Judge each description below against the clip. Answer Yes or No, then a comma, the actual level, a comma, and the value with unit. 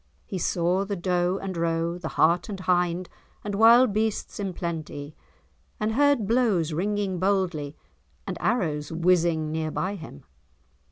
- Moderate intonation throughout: Yes, average, 3.5 semitones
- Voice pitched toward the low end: No, medium, 180 Hz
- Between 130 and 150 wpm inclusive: Yes, average, 145 wpm